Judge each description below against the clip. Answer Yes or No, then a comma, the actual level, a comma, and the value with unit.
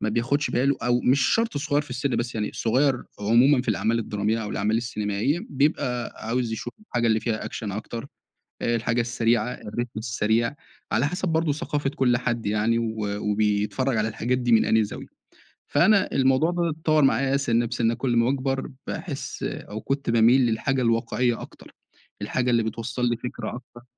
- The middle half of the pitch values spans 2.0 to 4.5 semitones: Yes, average, 3.1 semitones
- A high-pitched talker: No, low, 120 Hz